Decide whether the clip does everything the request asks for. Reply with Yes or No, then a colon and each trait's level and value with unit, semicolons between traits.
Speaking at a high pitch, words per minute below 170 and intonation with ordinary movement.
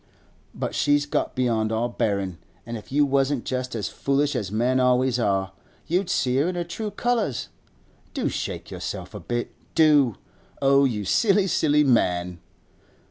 No: low, 130 Hz; average, 160 wpm; average, 4.7 semitones